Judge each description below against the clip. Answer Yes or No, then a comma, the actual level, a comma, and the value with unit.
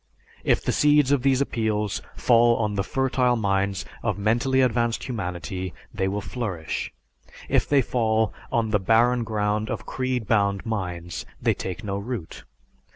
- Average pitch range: Yes, average, 3.7 semitones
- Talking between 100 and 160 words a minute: Yes, average, 155 wpm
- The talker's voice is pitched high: No, low, 110 Hz